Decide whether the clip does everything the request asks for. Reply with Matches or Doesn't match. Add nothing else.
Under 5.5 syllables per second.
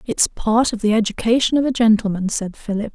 Doesn't match